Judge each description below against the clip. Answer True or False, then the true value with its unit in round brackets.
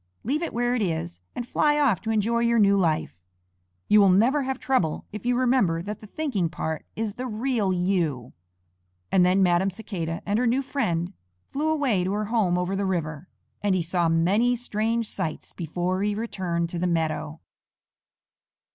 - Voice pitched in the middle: False (200 Hz)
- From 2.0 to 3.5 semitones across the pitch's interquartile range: False (5.3 semitones)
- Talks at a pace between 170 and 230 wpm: True (180 wpm)